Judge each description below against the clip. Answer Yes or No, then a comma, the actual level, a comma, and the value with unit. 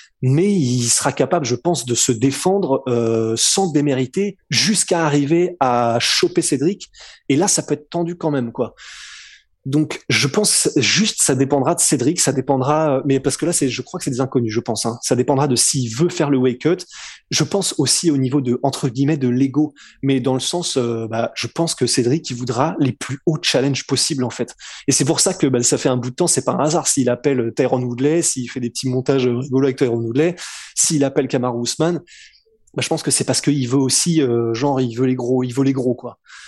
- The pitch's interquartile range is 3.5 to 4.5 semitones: Yes, average, 4.0 semitones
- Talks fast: Yes, fast, 230 wpm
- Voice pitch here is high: No, low, 135 Hz